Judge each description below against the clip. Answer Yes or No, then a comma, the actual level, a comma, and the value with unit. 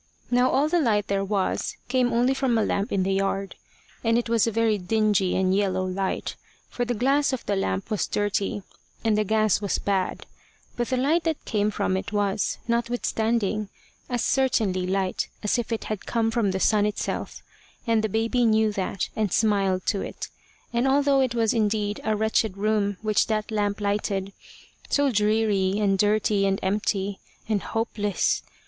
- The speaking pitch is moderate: No, high, 215 Hz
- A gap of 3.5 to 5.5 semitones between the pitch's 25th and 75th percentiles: No, average, 2.8 semitones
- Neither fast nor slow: Yes, average, 180 wpm